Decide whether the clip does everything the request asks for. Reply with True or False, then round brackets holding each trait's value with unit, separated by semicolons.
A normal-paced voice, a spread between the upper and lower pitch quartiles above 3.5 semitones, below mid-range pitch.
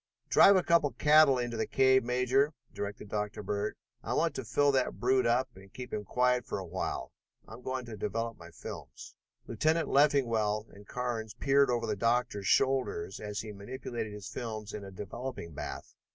True (185 wpm; 4.0 semitones; 120 Hz)